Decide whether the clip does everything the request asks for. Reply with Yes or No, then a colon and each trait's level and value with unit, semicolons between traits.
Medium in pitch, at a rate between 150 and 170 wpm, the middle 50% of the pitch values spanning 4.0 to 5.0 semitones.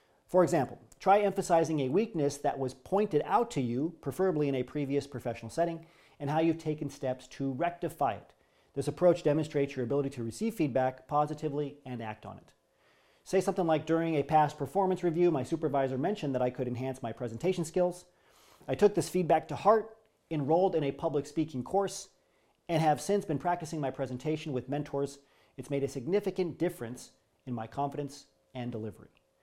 No: medium, 150 Hz; average, 180 wpm; average, 4.4 semitones